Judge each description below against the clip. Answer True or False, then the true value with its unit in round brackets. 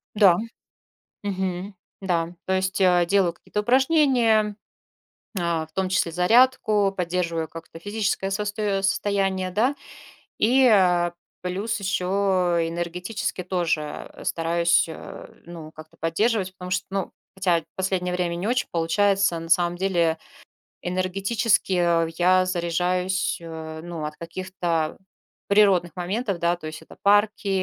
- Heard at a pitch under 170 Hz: False (185 Hz)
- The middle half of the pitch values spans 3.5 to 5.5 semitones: False (2.8 semitones)